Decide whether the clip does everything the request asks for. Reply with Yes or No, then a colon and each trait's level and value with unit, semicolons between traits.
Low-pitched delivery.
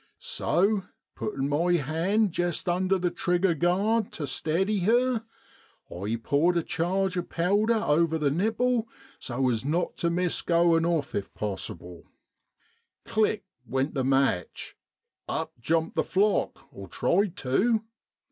No: medium, 175 Hz